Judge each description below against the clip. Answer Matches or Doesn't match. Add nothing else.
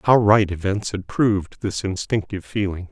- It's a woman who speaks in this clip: Doesn't match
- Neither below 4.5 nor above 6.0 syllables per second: Matches